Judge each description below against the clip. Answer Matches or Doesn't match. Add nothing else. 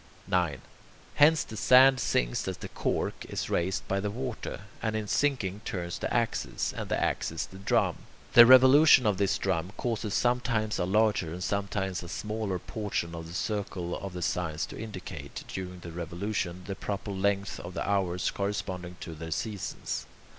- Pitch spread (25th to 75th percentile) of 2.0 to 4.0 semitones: Matches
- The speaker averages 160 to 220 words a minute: Matches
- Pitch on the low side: Matches